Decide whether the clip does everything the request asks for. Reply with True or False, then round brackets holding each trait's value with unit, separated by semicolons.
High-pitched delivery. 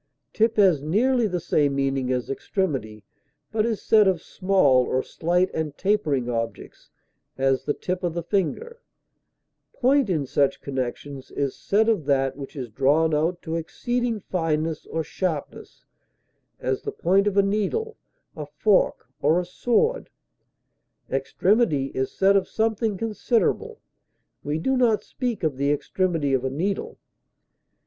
False (170 Hz)